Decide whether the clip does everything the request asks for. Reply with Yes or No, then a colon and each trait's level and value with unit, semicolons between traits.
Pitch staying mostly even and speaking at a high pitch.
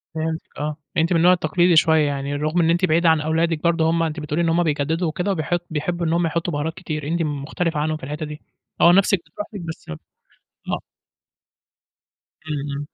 No: narrow, 2.1 semitones; medium, 160 Hz